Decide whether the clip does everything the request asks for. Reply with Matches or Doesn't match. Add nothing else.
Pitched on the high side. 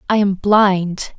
Matches